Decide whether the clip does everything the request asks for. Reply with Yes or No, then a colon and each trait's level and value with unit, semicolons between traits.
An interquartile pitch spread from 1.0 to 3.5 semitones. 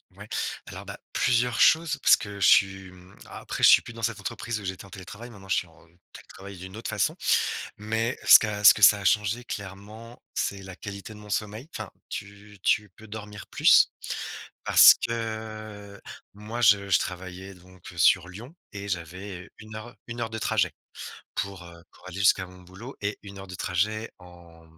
Yes: average, 2.7 semitones